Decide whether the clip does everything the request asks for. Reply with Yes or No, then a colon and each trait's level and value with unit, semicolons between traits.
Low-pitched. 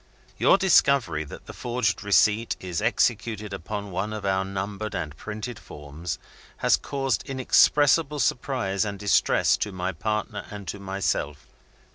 Yes: low, 105 Hz